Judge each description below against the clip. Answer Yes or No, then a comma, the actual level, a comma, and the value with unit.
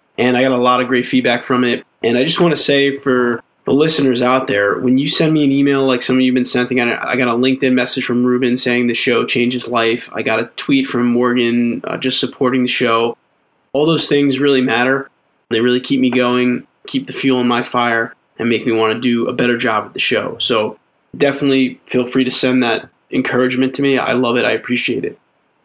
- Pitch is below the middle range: Yes, low, 125 Hz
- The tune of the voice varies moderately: No, narrow, 1.6 semitones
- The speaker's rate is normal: No, fast, 235 wpm